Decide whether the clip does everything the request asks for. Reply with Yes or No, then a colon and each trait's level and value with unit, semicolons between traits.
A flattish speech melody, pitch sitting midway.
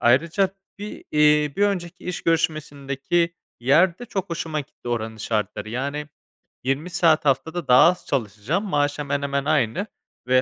No: average, 4.2 semitones; medium, 150 Hz